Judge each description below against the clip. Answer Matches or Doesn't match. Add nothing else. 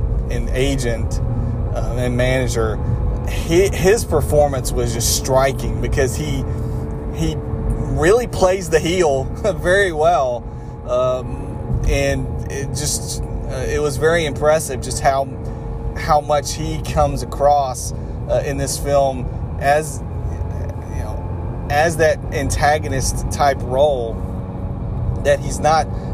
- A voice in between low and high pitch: Doesn't match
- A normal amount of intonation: Matches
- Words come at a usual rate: Doesn't match